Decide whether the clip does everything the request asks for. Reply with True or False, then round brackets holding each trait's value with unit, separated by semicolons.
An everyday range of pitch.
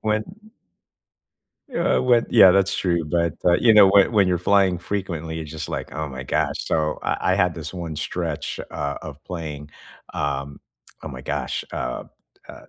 True (4.1 semitones)